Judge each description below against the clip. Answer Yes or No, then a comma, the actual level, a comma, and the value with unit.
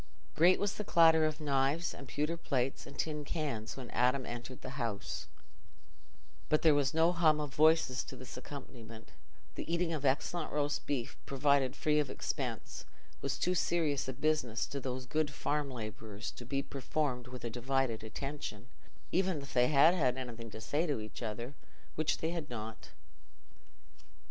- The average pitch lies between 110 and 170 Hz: Yes, medium, 140 Hz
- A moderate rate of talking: Yes, average, 170 wpm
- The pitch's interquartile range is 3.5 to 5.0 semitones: Yes, average, 3.8 semitones